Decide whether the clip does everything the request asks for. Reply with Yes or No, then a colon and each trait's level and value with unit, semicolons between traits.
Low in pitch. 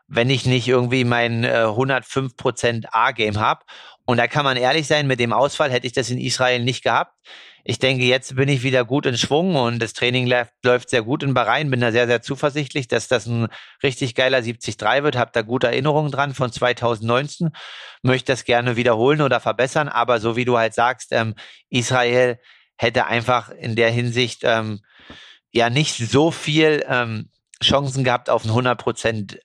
Yes: low, 125 Hz